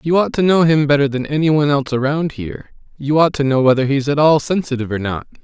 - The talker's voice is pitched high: No, medium, 145 Hz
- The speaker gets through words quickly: Yes, fast, 255 wpm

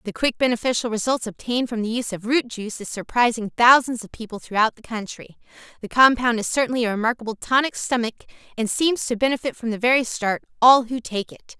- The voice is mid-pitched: No, high, 235 Hz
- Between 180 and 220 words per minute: Yes, average, 200 wpm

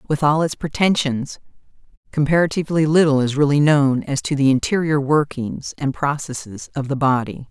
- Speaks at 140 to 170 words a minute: Yes, average, 150 wpm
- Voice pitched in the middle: Yes, medium, 145 Hz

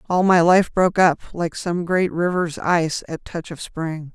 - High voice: No, medium, 170 Hz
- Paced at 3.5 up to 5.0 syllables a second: Yes, 4.6 syllables/s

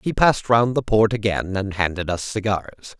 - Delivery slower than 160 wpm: No, average, 200 wpm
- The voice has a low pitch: Yes, low, 105 Hz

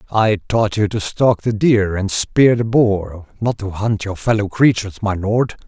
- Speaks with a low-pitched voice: Yes, low, 105 Hz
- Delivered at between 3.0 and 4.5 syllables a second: Yes, 4.3 syllables/s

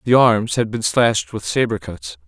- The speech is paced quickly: Yes, fast, 210 wpm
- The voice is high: No, low, 110 Hz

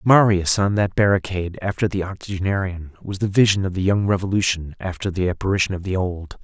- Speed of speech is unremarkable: Yes, average, 185 wpm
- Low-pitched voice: Yes, very low, 95 Hz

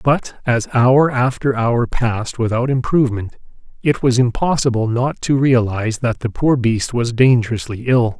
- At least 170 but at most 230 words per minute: No, average, 155 wpm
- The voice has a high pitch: No, low, 125 Hz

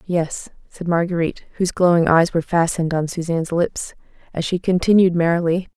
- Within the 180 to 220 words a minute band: No, average, 155 wpm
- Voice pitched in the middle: Yes, medium, 170 Hz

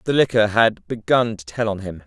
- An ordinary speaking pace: No, fast, 230 wpm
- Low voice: Yes, low, 110 Hz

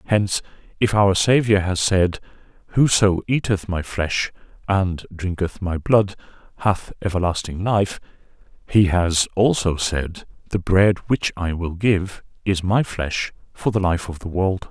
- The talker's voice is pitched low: Yes, very low, 95 Hz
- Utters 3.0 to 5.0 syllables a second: Yes, 4.1 syllables/s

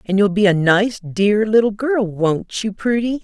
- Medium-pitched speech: No, high, 205 Hz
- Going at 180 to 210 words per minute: Yes, fast, 205 wpm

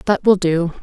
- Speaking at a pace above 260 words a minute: No, fast, 220 wpm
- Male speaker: No, female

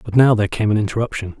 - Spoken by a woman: No, male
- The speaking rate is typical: No, fast, 255 wpm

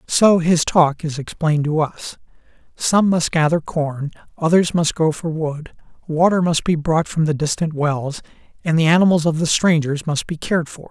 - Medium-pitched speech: Yes, medium, 160 Hz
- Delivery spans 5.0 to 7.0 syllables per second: No, 4.8 syllables/s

